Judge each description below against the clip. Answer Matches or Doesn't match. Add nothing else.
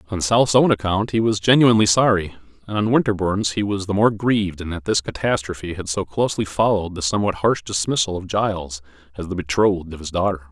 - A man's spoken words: Matches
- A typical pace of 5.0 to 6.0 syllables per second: Doesn't match